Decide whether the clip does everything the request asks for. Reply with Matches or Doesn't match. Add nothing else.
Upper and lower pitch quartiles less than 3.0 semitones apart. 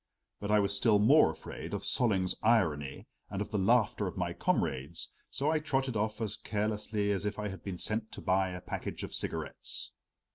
Matches